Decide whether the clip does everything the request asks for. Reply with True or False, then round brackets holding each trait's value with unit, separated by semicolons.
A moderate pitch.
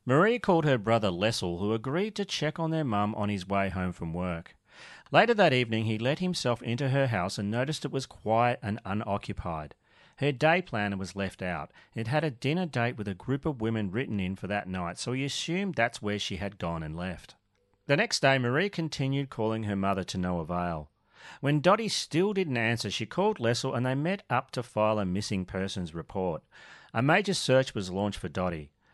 False (110 Hz)